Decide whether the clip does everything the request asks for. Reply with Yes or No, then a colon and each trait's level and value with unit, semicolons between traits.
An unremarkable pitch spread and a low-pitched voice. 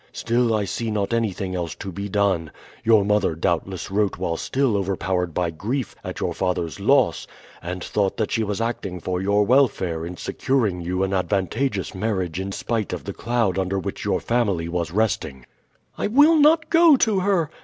Yes: average, 4.3 semitones; low, 100 Hz